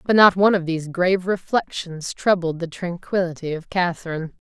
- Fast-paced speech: No, average, 165 wpm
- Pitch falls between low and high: Yes, medium, 175 Hz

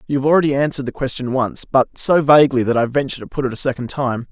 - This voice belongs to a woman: No, male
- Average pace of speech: No, fast, 265 wpm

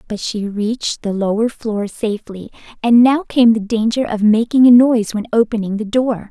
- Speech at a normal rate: Yes, average, 190 wpm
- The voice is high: Yes, high, 225 Hz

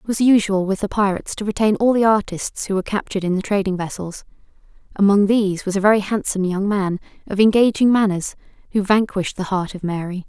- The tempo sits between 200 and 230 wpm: Yes, fast, 205 wpm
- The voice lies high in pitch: Yes, high, 200 Hz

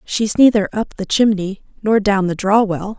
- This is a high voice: Yes, high, 205 Hz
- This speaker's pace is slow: No, average, 200 wpm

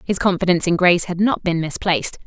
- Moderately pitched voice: Yes, medium, 180 Hz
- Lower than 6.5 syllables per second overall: No, 6.7 syllables/s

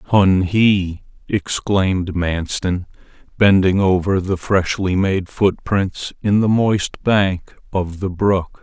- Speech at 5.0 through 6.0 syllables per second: No, 3.2 syllables/s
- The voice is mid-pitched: No, very low, 95 Hz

